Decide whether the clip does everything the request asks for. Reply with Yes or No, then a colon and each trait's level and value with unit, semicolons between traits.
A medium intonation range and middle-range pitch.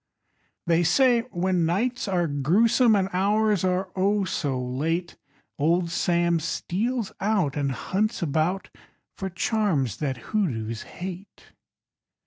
Yes: average, 4.4 semitones; medium, 180 Hz